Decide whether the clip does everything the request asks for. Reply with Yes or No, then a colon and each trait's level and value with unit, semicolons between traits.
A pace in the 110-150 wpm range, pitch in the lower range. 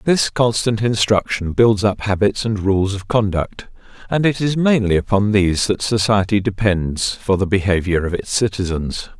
No: average, 165 wpm; low, 105 Hz